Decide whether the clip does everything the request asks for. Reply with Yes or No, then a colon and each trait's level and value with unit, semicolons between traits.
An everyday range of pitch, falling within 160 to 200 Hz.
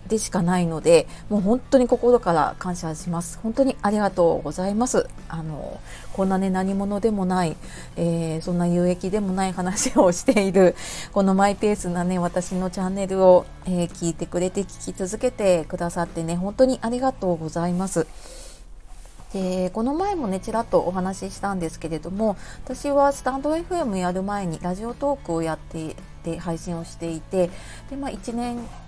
Yes: average, 4.3 semitones; medium, 185 Hz